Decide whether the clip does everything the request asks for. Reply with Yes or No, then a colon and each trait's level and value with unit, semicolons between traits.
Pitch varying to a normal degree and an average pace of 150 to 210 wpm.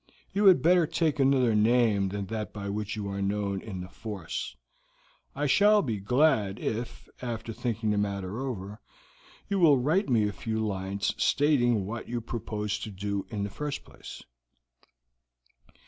Yes: average, 4.7 semitones; average, 165 wpm